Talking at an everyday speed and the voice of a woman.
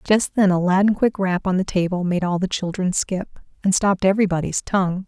No: fast, 225 wpm; female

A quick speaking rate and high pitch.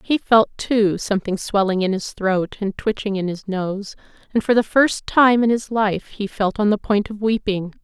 Yes: fast, 215 wpm; high, 205 Hz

